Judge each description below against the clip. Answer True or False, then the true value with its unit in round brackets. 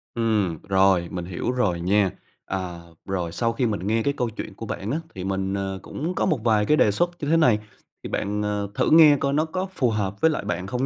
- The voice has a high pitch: False (105 Hz)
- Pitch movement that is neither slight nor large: True (4.8 semitones)